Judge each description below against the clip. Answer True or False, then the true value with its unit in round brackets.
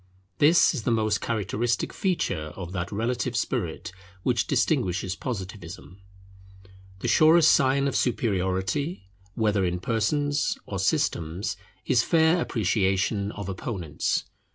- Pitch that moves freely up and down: True (5.7 semitones)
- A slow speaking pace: True (115 wpm)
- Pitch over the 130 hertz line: False (105 Hz)